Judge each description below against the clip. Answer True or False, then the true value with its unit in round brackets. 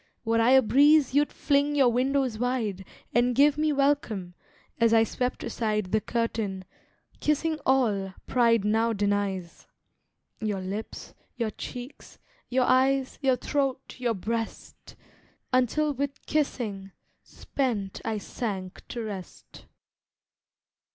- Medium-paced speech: False (120 wpm)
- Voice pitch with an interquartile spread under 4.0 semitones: False (4.3 semitones)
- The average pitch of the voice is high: True (235 Hz)